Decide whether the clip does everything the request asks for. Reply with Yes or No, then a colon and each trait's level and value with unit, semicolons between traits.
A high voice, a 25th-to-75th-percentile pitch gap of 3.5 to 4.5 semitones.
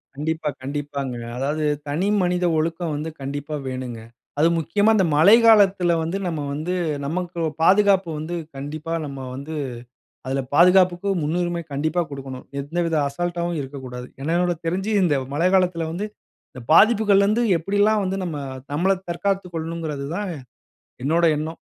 No: medium, 165 Hz; average, 3.9 semitones